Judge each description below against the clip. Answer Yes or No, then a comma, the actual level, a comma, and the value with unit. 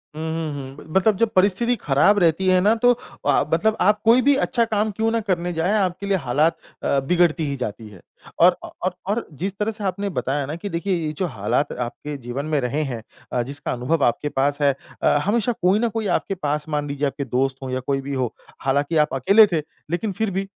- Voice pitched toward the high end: No, medium, 165 Hz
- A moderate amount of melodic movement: No, wide, 6.5 semitones